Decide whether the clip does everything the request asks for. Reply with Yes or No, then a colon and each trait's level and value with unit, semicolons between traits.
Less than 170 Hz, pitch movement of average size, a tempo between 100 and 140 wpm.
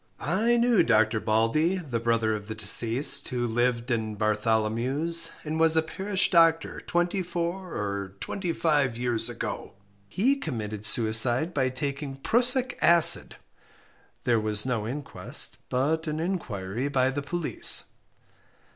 No: low, 135 Hz; wide, 7.0 semitones; slow, 135 wpm